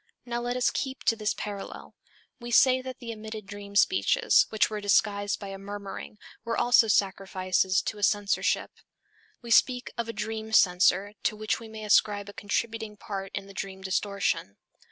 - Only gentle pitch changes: Yes, narrow, 2.3 semitones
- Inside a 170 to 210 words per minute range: Yes, average, 180 wpm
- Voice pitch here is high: Yes, high, 210 Hz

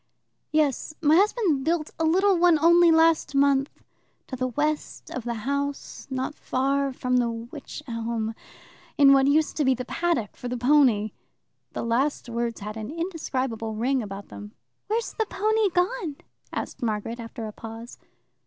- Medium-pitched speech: No, very high, 275 Hz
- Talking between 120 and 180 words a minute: Yes, average, 160 wpm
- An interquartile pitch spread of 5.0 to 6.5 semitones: Yes, wide, 5.5 semitones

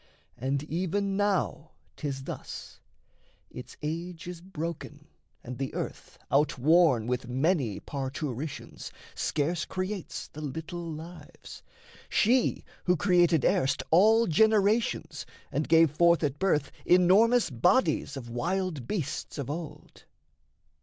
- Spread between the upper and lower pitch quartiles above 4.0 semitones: Yes, average, 4.7 semitones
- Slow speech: Yes, slow, 110 wpm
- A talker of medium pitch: Yes, medium, 160 Hz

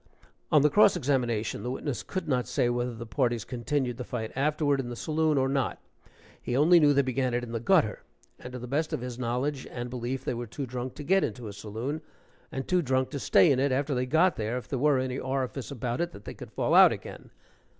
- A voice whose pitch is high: No, low, 130 Hz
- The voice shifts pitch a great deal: No, average, 3.1 semitones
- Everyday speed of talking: No, fast, 245 wpm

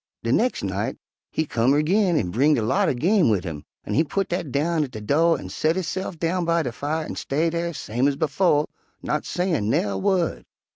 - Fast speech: Yes, fast, 220 wpm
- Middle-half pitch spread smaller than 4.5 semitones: No, average, 5.3 semitones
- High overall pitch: No, medium, 155 Hz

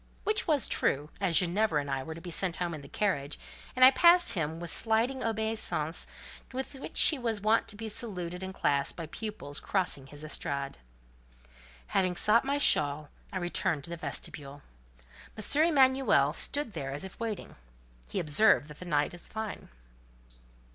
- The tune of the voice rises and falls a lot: Yes, wide, 6.9 semitones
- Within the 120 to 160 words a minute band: No, average, 175 wpm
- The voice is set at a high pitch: No, medium, 180 Hz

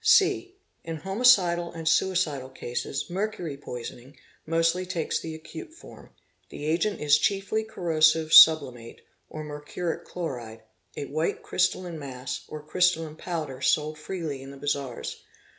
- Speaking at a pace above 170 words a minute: No, average, 140 wpm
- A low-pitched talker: No, medium, 160 Hz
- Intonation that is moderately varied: Yes, average, 4.0 semitones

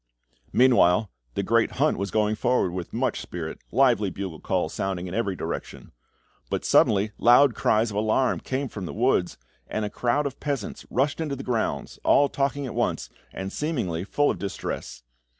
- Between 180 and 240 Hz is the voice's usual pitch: No, low, 110 Hz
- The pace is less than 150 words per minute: No, average, 175 wpm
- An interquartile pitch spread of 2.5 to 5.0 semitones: No, wide, 5.5 semitones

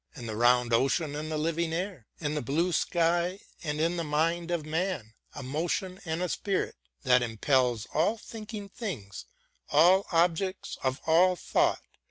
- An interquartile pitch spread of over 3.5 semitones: Yes, average, 4.7 semitones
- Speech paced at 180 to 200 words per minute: No, average, 165 wpm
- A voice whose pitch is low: No, medium, 160 Hz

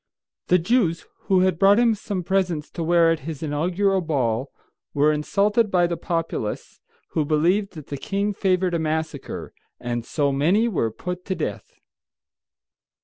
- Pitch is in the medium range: Yes, medium, 170 Hz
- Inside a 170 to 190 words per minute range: No, average, 155 wpm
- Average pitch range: Yes, average, 4.2 semitones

